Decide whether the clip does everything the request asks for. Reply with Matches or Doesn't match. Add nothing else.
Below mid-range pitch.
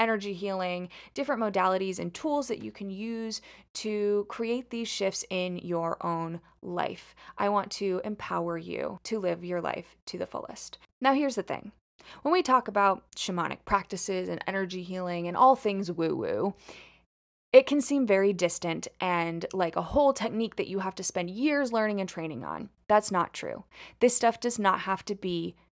Doesn't match